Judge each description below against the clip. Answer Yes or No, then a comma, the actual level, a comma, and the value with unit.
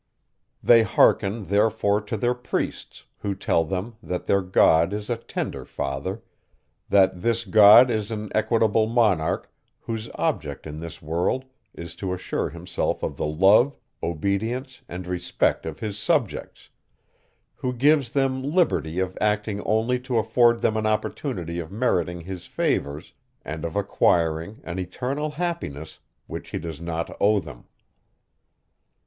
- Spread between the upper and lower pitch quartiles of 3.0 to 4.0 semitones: No, average, 5.1 semitones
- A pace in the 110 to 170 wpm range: Yes, average, 140 wpm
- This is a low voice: Yes, low, 100 Hz